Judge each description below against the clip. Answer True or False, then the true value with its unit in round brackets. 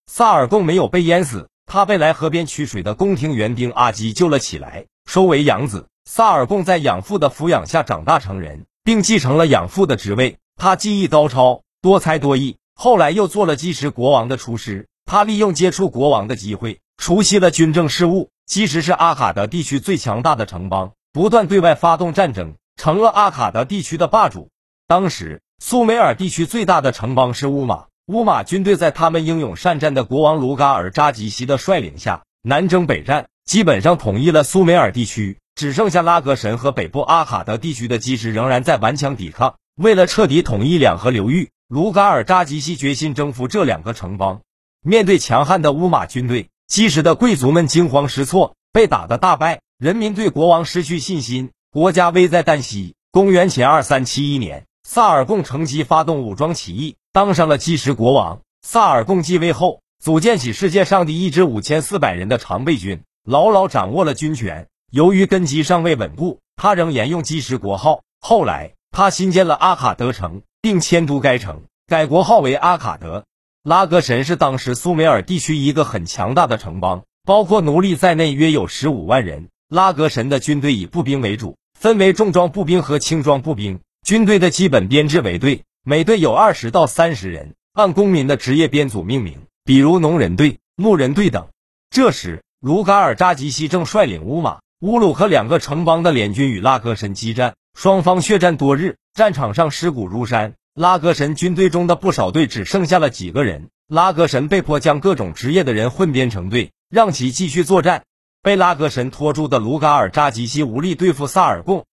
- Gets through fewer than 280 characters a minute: False (295 characters per minute)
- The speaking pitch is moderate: True (155 Hz)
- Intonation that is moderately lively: False (6.0 semitones)